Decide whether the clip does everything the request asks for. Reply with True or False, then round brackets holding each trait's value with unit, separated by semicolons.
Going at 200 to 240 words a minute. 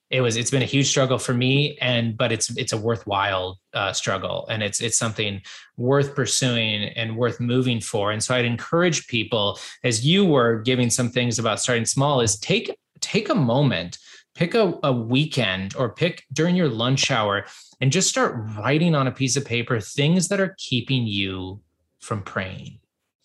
False (185 wpm)